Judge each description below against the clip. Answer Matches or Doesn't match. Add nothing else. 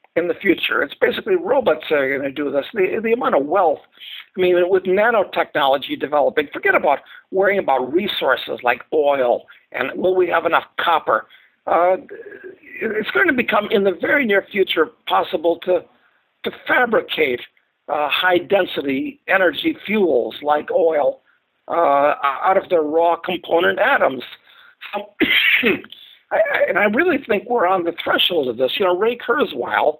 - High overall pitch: Matches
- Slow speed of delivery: Doesn't match